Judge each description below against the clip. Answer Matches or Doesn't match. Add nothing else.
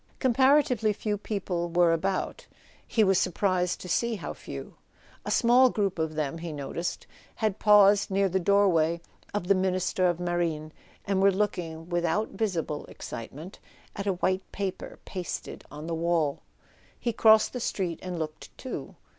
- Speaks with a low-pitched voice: Doesn't match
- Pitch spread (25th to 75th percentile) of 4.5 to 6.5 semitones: Doesn't match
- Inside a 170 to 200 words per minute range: Doesn't match